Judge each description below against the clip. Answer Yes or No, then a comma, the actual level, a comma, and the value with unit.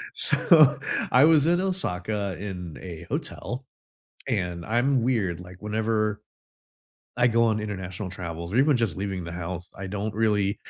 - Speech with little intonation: No, average, 4.5 semitones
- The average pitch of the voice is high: No, low, 105 Hz